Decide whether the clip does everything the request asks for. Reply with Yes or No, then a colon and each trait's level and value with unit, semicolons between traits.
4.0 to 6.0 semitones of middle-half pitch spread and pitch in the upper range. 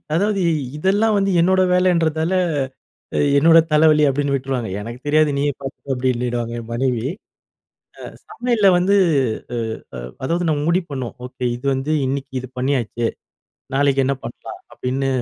No: average, 4.8 semitones; medium, 140 Hz